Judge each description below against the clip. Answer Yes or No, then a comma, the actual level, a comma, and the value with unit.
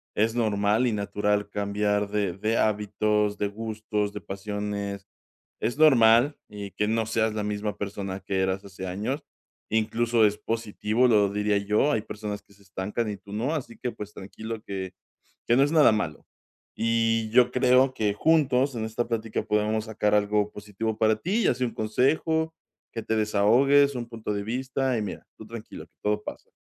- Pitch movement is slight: Yes, narrow, 2.2 semitones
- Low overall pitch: Yes, low, 110 Hz